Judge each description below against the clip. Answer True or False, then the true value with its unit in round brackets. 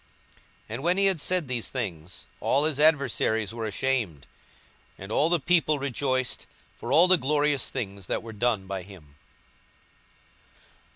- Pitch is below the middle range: True (130 Hz)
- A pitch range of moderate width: False (6.4 semitones)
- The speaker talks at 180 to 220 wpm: False (155 wpm)